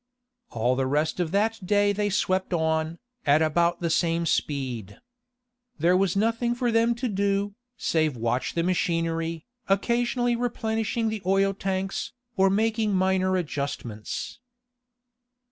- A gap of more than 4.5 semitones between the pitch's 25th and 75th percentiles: Yes, average, 4.9 semitones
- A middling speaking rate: No, slow, 130 wpm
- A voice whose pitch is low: No, medium, 185 Hz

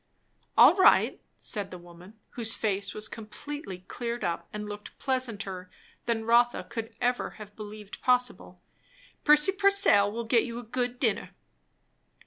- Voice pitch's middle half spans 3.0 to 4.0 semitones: Yes, average, 3.3 semitones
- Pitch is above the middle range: Yes, high, 225 Hz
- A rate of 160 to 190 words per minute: No, average, 140 wpm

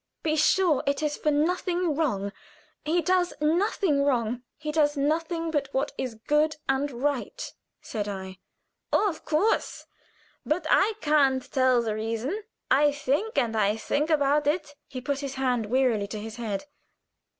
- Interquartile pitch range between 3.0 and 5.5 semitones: Yes, average, 3.9 semitones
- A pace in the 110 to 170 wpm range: Yes, average, 155 wpm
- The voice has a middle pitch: No, very high, 290 Hz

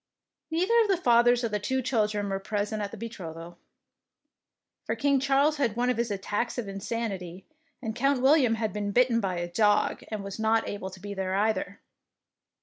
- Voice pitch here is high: Yes, high, 220 Hz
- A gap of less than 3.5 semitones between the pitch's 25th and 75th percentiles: No, average, 3.8 semitones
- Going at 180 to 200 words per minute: Yes, average, 190 wpm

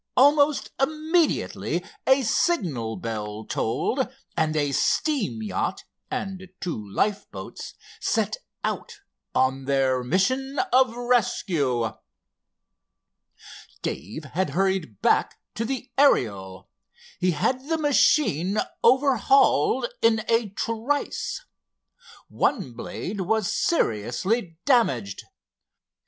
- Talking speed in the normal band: No, slow, 90 wpm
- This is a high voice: Yes, high, 195 Hz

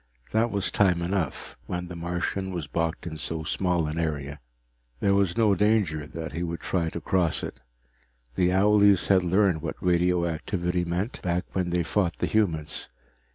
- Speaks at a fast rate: No, average, 170 wpm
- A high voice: No, very low, 90 Hz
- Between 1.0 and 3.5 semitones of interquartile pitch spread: Yes, average, 2.7 semitones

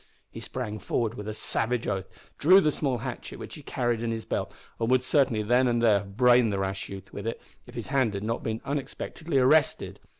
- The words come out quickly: Yes, fast, 225 wpm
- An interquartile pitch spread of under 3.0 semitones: No, average, 3.4 semitones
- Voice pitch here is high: No, low, 115 Hz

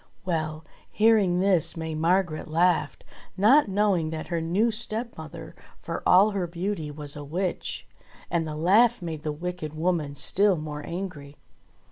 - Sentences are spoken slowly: No, average, 145 wpm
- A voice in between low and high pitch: Yes, medium, 170 Hz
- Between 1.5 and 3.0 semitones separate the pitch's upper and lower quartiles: No, average, 3.9 semitones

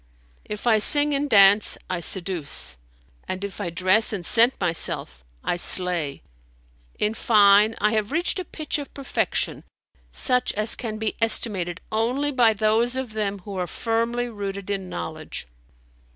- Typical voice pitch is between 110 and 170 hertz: No, high, 215 Hz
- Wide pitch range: No, average, 3.8 semitones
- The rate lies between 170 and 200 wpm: No, average, 150 wpm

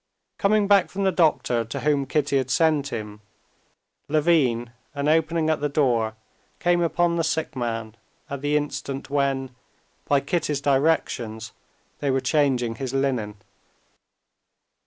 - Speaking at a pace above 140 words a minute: No, slow, 135 wpm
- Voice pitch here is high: No, medium, 140 Hz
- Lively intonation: No, average, 4.2 semitones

